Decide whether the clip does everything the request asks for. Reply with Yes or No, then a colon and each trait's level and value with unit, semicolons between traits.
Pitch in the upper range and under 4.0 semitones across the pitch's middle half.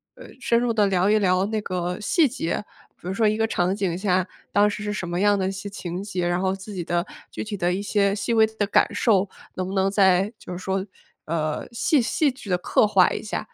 Yes: high, 195 Hz; narrow, 2.6 semitones